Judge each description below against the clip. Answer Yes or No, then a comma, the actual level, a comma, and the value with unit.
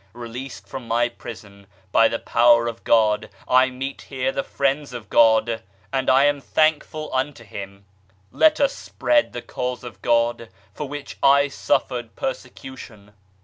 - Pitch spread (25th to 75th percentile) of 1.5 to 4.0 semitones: Yes, average, 3.0 semitones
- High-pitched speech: No, low, 125 Hz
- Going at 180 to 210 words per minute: No, average, 150 wpm